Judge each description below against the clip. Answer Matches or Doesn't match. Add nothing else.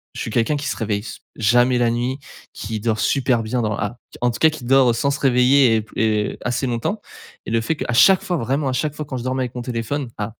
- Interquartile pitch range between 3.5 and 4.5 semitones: Doesn't match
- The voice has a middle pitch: Doesn't match